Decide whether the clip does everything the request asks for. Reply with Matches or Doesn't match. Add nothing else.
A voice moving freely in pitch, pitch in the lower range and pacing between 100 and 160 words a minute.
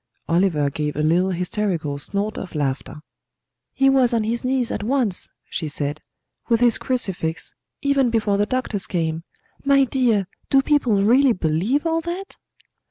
Doesn't match